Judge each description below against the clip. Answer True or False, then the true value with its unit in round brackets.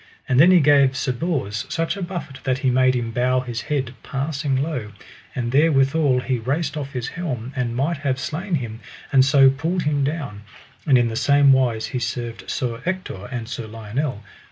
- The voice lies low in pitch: True (130 Hz)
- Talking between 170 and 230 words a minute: True (195 wpm)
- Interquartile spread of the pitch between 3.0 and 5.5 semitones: True (3.4 semitones)